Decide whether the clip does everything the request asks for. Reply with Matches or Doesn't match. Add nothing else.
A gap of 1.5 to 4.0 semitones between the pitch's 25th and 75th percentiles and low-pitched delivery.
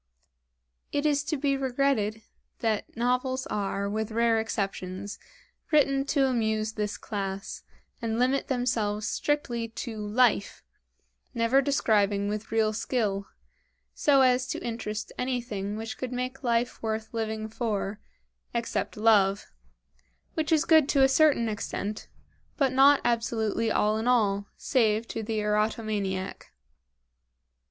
Doesn't match